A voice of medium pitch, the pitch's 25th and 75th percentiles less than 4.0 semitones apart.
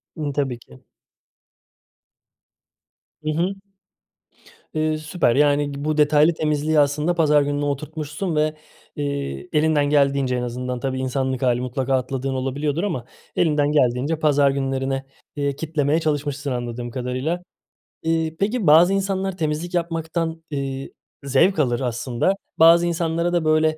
Yes: medium, 145 Hz; average, 3.3 semitones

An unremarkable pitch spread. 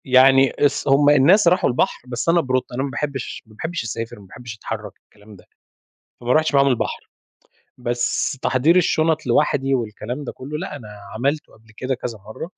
Yes: average, 3.7 semitones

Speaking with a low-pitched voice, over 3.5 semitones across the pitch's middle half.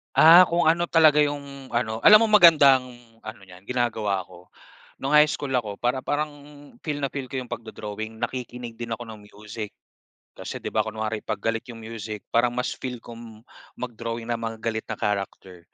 Yes: low, 120 Hz; average, 4.0 semitones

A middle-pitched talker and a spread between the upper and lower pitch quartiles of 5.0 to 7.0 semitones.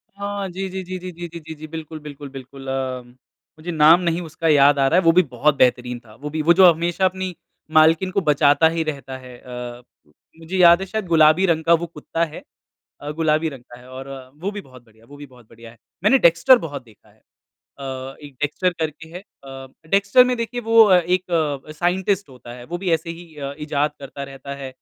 No: medium, 155 Hz; average, 4.6 semitones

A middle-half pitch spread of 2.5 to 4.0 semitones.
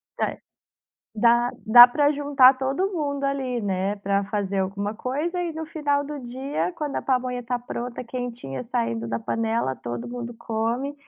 No: average, 5.3 semitones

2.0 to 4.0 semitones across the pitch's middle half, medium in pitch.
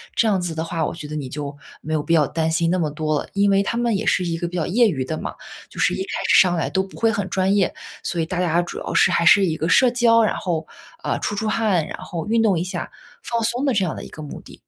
No: average, 4.5 semitones; medium, 180 Hz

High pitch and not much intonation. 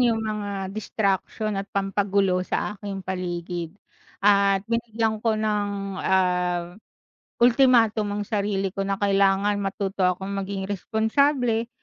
Yes: high, 200 Hz; narrow, 2.1 semitones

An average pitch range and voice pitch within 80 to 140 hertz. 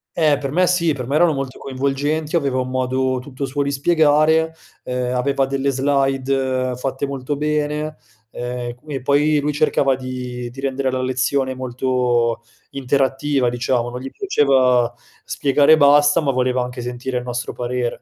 No: narrow, 2.3 semitones; low, 135 Hz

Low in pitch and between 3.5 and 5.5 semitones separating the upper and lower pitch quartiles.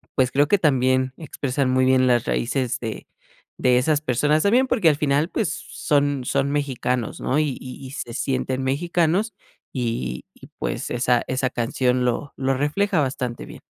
No: low, 130 Hz; average, 2.8 semitones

